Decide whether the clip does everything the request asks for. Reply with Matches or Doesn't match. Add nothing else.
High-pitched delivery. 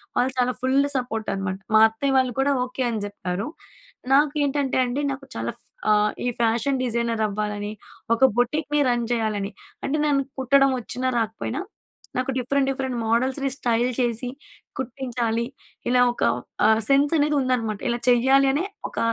Matches